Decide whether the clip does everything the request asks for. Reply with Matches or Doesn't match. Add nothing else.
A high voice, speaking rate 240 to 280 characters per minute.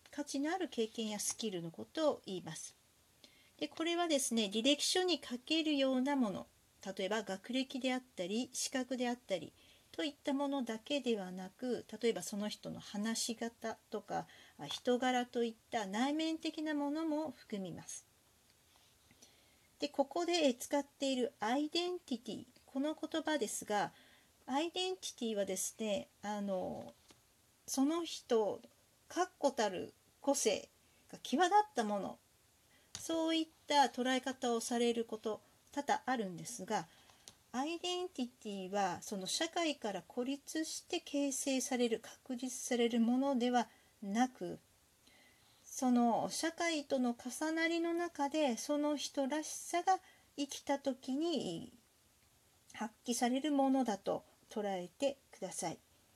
Matches